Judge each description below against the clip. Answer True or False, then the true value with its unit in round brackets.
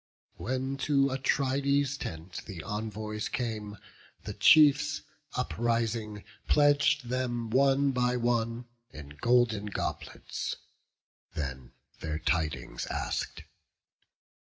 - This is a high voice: False (120 Hz)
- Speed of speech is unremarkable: False (90 wpm)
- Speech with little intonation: False (4.6 semitones)